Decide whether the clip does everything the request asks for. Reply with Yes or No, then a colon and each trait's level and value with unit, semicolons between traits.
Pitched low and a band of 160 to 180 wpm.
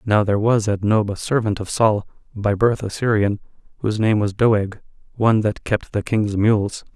No: low, 105 Hz; average, 200 wpm